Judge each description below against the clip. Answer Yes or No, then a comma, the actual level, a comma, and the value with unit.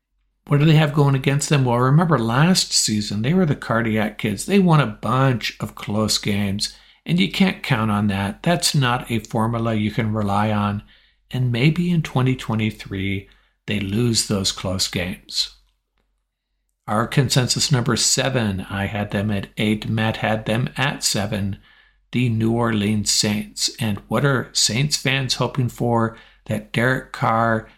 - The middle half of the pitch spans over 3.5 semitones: Yes, average, 4.2 semitones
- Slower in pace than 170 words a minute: Yes, average, 160 wpm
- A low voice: Yes, low, 115 Hz